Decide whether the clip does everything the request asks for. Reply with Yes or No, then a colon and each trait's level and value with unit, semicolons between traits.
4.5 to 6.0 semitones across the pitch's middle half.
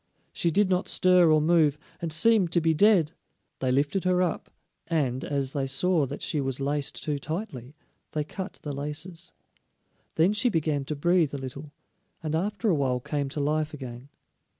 No: average, 3.9 semitones